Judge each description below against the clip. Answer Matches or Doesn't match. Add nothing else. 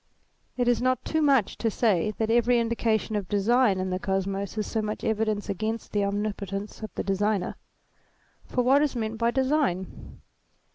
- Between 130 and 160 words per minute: Doesn't match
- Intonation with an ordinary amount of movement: Matches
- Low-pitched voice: Doesn't match